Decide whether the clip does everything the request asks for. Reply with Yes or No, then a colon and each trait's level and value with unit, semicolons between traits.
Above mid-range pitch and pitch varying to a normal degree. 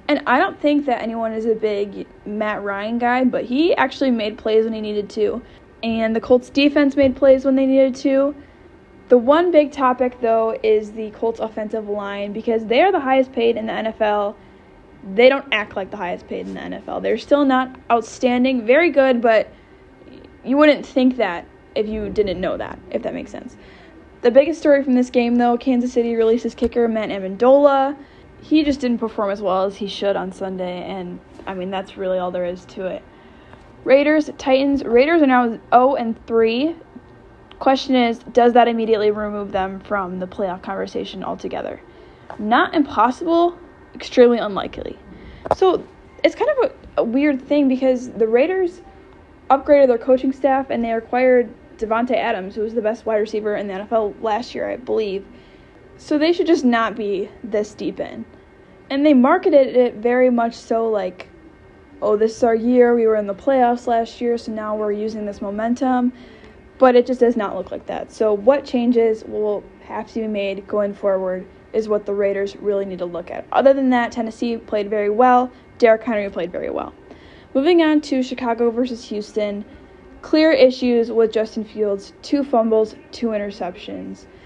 Yes: high, 230 Hz; average, 3.8 semitones